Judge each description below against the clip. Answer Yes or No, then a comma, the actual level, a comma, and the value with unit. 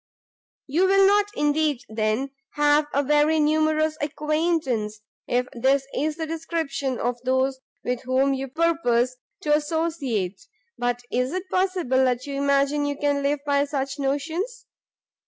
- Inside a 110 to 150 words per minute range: Yes, slow, 135 wpm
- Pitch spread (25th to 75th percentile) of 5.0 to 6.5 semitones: No, average, 3.2 semitones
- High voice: Yes, very high, 285 Hz